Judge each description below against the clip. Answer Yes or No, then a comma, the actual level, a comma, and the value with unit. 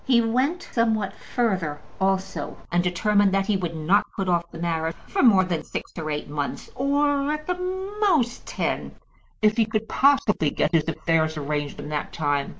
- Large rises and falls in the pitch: Yes, wide, 6.5 semitones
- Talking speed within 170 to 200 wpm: Yes, average, 180 wpm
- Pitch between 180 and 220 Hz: Yes, high, 190 Hz